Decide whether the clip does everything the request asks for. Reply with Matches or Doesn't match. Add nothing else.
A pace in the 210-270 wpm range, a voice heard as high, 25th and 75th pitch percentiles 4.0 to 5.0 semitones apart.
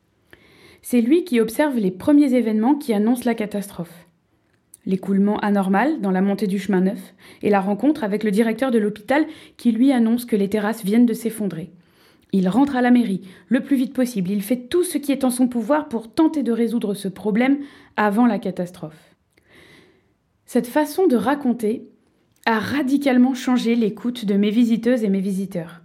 Doesn't match